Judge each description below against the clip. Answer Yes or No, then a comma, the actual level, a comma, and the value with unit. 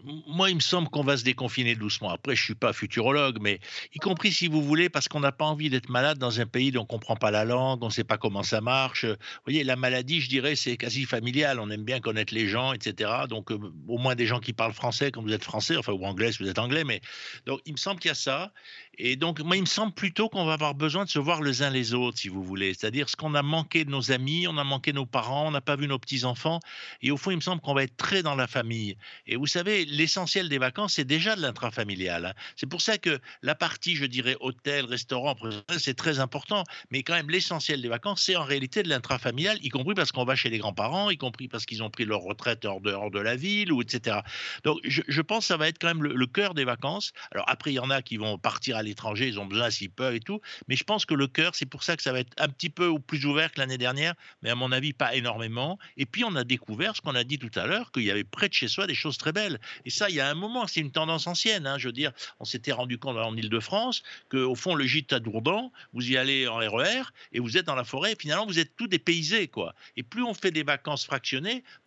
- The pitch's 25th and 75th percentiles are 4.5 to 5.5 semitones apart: Yes, average, 5.2 semitones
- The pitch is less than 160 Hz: Yes, low, 135 Hz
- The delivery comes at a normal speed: No, fast, 280 wpm